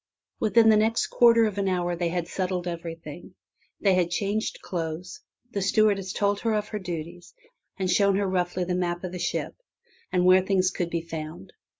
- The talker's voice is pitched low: No, medium, 185 Hz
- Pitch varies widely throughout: No, narrow, 2.5 semitones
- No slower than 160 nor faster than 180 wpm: No, average, 195 wpm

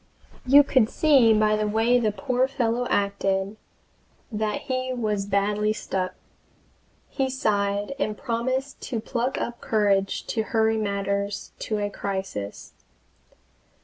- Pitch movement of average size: Yes, average, 3.5 semitones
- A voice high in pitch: Yes, high, 215 Hz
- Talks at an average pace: No, slow, 125 wpm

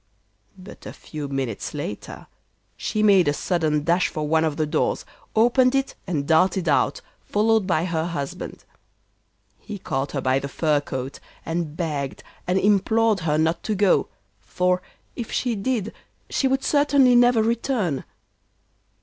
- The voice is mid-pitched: Yes, medium, 175 Hz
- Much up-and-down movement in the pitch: Yes, wide, 6.4 semitones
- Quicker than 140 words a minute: Yes, average, 150 wpm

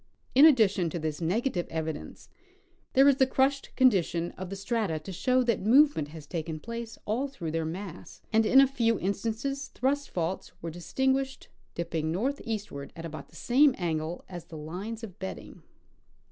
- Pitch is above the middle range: Yes, high, 195 Hz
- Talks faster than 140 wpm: Yes, average, 175 wpm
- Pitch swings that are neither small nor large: No, wide, 7.8 semitones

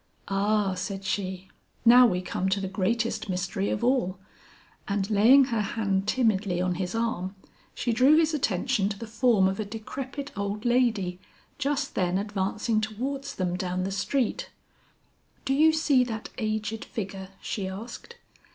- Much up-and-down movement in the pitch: No, average, 4.1 semitones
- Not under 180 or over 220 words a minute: No, average, 155 wpm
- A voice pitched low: No, high, 210 Hz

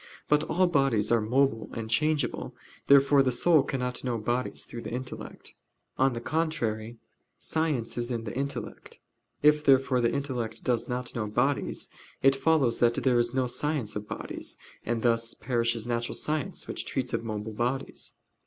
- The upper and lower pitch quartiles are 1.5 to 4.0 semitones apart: Yes, average, 3.0 semitones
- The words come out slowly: No, average, 165 wpm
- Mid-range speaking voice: No, low, 125 Hz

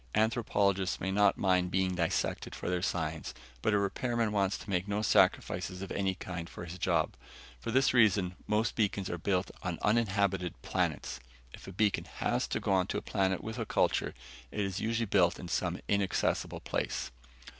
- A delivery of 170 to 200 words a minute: Yes, average, 180 wpm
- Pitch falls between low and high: No, very low, 95 Hz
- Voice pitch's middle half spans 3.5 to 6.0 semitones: No, narrow, 2.6 semitones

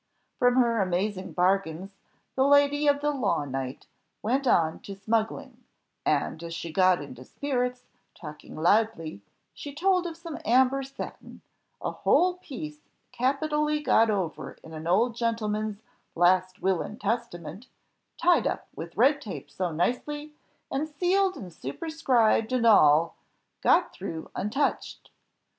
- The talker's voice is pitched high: Yes, high, 225 Hz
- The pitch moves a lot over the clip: Yes, wide, 8.1 semitones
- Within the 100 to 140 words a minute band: Yes, slow, 135 wpm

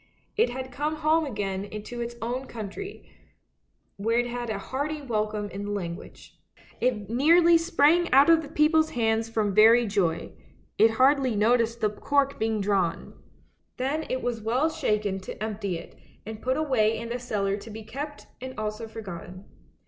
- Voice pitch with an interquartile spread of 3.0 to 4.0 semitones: No, average, 4.6 semitones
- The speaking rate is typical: Yes, average, 170 wpm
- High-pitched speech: Yes, high, 230 Hz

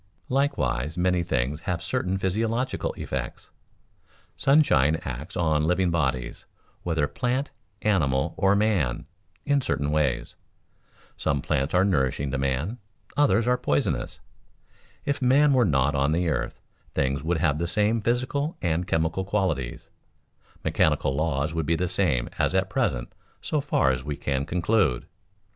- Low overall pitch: Yes, very low, 85 Hz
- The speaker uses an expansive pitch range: Yes, wide, 7.2 semitones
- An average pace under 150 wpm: Yes, average, 140 wpm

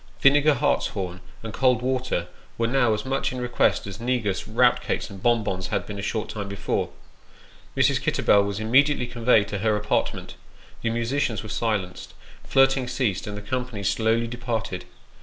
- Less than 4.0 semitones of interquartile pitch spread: Yes, average, 3.5 semitones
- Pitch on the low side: Yes, low, 115 Hz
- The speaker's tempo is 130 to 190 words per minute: Yes, average, 170 wpm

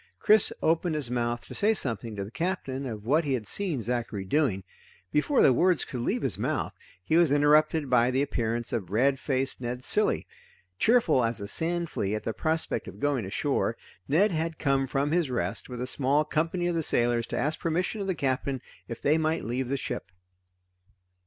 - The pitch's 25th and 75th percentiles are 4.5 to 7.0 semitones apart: Yes, average, 5.2 semitones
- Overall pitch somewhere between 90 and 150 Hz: Yes, low, 135 Hz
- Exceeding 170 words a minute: Yes, average, 200 wpm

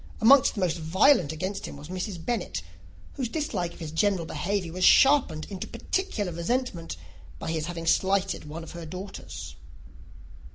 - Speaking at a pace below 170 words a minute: Yes, average, 160 wpm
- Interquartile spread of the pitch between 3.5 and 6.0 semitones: Yes, average, 3.9 semitones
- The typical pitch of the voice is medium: Yes, medium, 180 Hz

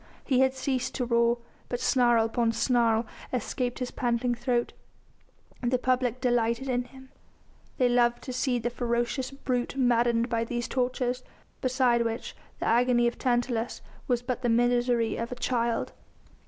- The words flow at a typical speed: Yes, average, 155 wpm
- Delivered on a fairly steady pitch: Yes, narrow, 1.2 semitones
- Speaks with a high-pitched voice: Yes, high, 245 Hz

